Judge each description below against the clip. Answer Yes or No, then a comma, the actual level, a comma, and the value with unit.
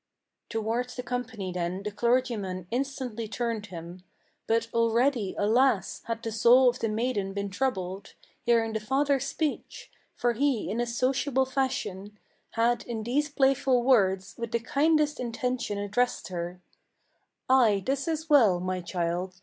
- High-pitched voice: Yes, high, 230 Hz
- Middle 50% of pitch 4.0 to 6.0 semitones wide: Yes, average, 4.3 semitones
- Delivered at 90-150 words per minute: Yes, average, 145 wpm